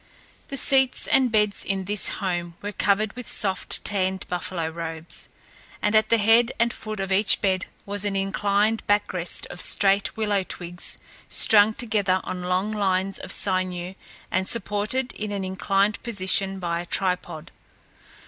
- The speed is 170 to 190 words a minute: No, average, 160 wpm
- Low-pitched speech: No, high, 195 Hz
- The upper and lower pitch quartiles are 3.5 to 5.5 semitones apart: No, narrow, 2.4 semitones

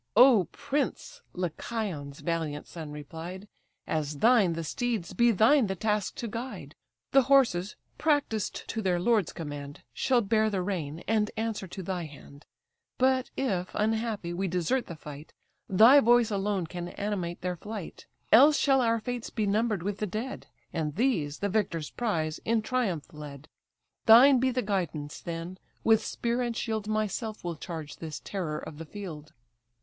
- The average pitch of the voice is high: Yes, high, 200 Hz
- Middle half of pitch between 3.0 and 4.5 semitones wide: No, wide, 5.6 semitones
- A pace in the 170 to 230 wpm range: No, average, 160 wpm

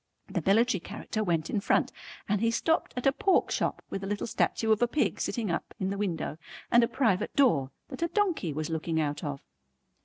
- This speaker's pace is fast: Yes, fast, 215 wpm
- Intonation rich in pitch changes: Yes, wide, 6.4 semitones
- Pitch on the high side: Yes, high, 205 Hz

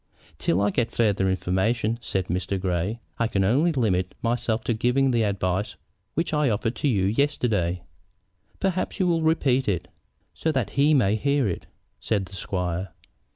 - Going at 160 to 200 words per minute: Yes, average, 165 wpm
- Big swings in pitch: Yes, wide, 6.0 semitones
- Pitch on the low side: Yes, low, 110 Hz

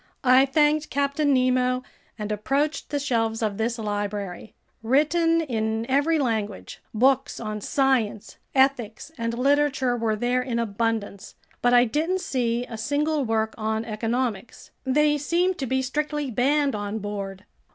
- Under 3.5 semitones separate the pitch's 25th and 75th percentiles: No, average, 4.3 semitones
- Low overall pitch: No, very high, 250 Hz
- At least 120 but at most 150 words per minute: Yes, average, 140 wpm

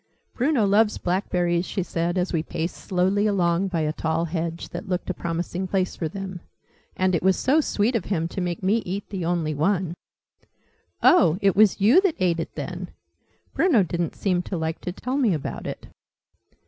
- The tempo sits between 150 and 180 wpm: No, average, 190 wpm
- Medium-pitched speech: Yes, medium, 180 Hz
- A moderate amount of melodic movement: Yes, average, 3.0 semitones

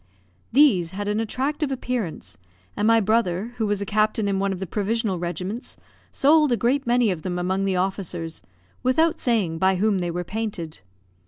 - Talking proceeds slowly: No, average, 180 wpm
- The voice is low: No, high, 205 Hz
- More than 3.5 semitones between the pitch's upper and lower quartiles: Yes, average, 4.4 semitones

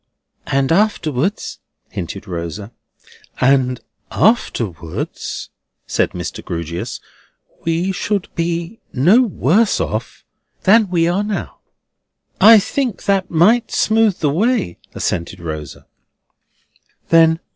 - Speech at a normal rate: No, slow, 95 wpm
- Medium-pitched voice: Yes, medium, 170 Hz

